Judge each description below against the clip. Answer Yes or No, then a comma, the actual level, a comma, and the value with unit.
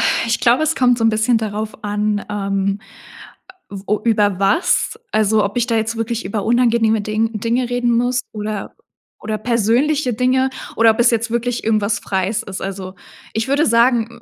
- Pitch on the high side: Yes, high, 225 Hz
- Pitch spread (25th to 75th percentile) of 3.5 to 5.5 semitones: No, narrow, 2.4 semitones